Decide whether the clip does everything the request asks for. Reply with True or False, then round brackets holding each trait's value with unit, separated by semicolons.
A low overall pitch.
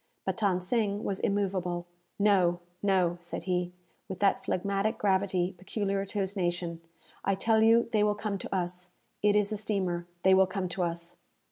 False (190 Hz)